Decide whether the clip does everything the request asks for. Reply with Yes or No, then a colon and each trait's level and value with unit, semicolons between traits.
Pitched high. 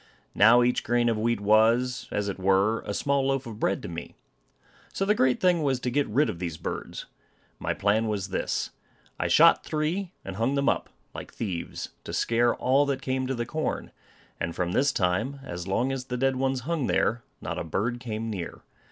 No: low, 120 Hz